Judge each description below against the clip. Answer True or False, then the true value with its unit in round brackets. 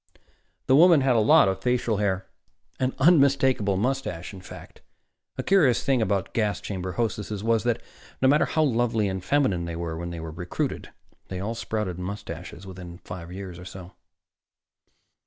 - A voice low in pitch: True (100 Hz)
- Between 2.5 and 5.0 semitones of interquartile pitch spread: False (5.4 semitones)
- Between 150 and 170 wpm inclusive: True (160 wpm)